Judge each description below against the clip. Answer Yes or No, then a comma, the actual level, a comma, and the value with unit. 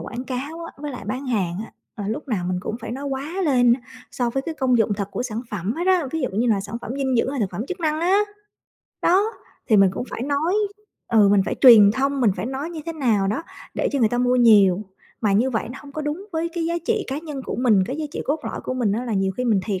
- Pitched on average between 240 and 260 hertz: Yes, very high, 250 Hz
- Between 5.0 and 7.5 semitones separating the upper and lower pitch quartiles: Yes, average, 5.3 semitones